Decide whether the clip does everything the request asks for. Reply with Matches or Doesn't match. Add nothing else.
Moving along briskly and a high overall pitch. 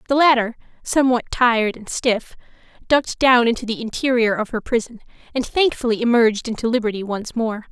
Doesn't match